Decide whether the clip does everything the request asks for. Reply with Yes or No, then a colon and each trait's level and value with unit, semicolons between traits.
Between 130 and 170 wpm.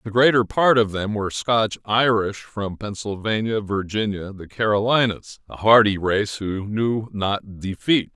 Yes: average, 140 wpm